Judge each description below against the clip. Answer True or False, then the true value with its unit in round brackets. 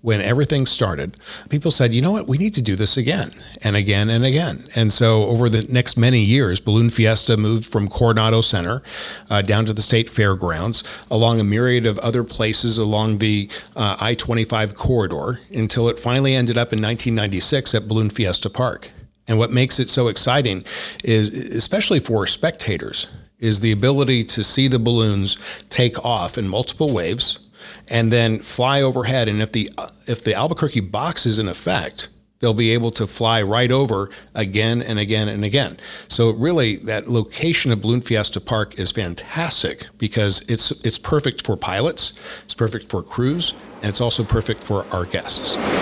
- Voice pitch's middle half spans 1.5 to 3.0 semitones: True (2.4 semitones)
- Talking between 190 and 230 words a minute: False (175 wpm)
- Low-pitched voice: True (115 Hz)